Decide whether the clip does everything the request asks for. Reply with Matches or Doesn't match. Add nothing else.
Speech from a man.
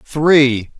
Matches